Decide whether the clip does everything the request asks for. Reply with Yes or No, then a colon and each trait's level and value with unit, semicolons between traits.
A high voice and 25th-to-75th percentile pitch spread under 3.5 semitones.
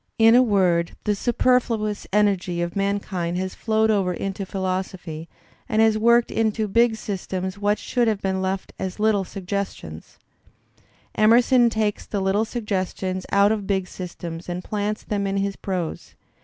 Yes: high, 200 Hz; narrow, 2.6 semitones